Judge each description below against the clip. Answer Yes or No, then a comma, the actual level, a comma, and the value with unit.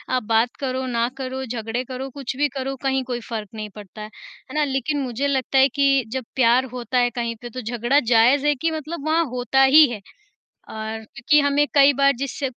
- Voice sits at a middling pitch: No, very high, 260 Hz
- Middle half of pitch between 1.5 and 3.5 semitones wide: Yes, average, 2.8 semitones